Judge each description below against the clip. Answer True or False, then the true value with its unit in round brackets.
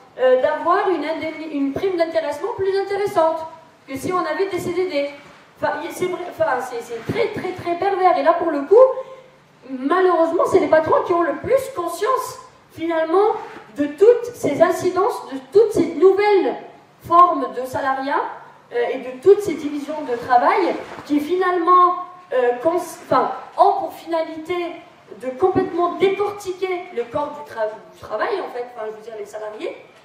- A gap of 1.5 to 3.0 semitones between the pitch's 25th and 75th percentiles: False (4.6 semitones)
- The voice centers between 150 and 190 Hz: False (345 Hz)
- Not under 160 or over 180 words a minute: True (170 wpm)